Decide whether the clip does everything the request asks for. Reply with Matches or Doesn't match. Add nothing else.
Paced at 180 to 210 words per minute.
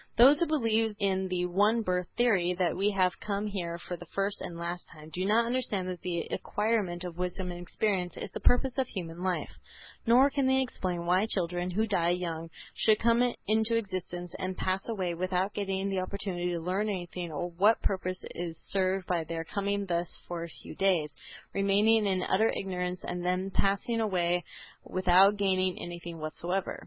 Matches